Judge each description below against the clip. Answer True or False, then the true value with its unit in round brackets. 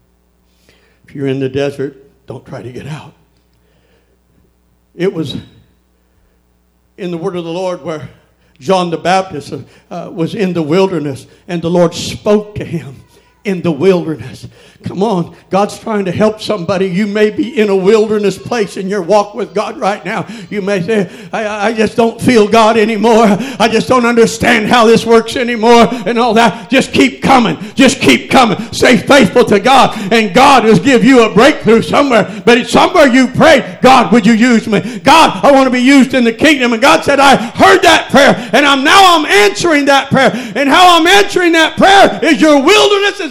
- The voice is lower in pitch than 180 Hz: False (215 Hz)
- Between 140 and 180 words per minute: False (190 wpm)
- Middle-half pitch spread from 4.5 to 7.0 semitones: True (5.4 semitones)